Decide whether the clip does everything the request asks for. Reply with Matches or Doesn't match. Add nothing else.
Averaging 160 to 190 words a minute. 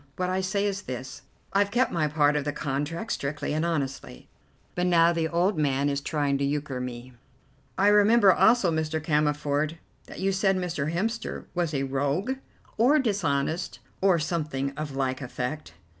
Matches